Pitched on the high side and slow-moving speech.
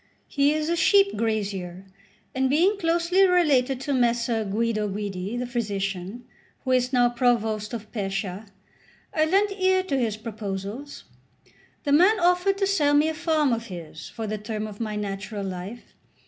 No: high, 240 Hz; average, 160 wpm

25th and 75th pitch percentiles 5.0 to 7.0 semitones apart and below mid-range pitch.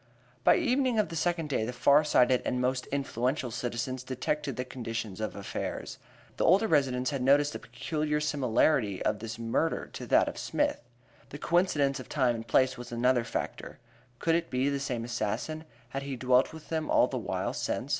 No: average, 3.7 semitones; low, 130 Hz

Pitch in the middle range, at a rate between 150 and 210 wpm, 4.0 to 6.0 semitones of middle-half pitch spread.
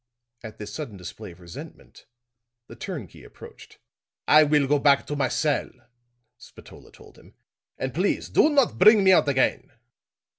Yes: medium, 145 Hz; average, 155 wpm; wide, 5.6 semitones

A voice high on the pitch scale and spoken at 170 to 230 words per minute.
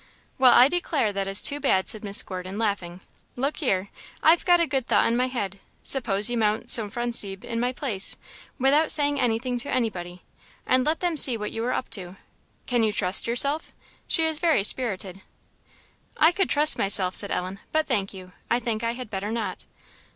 Yes: high, 230 Hz; average, 190 wpm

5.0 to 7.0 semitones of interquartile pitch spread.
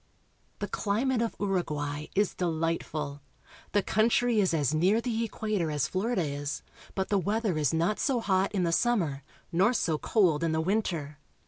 Yes: wide, 5.6 semitones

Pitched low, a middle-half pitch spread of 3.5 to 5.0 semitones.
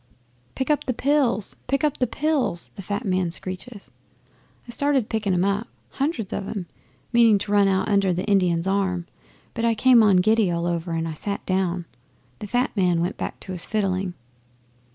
No: high, 200 Hz; average, 4.1 semitones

